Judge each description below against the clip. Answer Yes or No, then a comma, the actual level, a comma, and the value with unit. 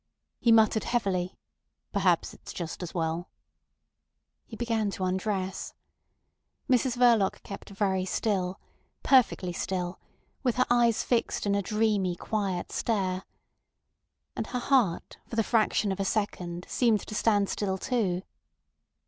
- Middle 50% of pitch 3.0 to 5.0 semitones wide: Yes, average, 3.6 semitones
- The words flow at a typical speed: No, slow, 130 wpm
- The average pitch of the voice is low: No, high, 200 Hz